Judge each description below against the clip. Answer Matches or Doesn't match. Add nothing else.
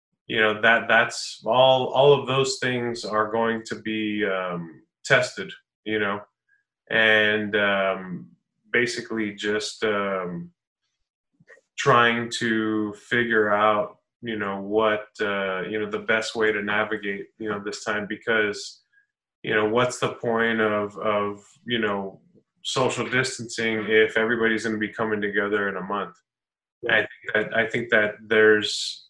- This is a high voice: Doesn't match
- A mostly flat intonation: Matches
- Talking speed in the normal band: Matches